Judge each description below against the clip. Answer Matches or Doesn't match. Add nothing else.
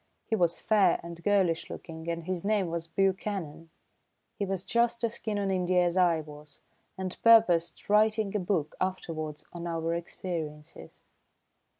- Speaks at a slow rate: Doesn't match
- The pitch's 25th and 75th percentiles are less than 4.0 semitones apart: Matches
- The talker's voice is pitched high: Doesn't match